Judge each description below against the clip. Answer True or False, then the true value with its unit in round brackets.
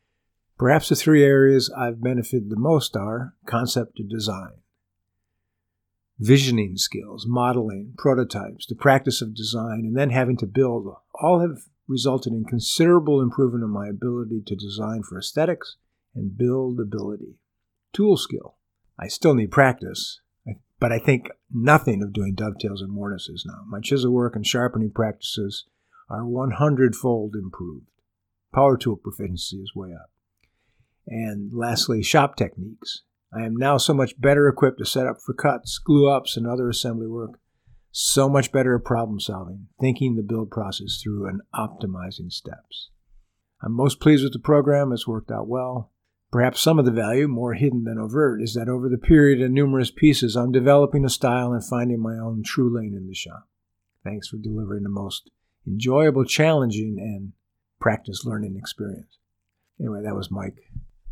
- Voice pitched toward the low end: True (115 Hz)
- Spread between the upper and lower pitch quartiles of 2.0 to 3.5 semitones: False (4.3 semitones)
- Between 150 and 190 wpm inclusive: True (160 wpm)